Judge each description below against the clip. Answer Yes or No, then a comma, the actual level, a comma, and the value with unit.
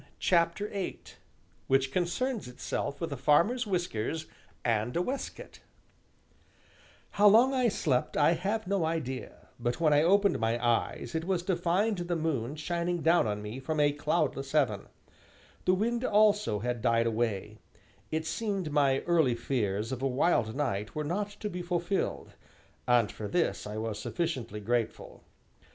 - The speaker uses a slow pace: No, average, 155 wpm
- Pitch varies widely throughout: Yes, wide, 7.0 semitones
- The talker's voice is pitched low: No, medium, 155 Hz